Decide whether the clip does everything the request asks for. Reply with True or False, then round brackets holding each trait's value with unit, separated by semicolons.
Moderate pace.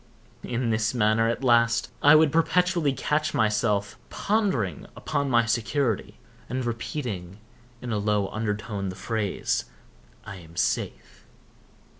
False (125 wpm)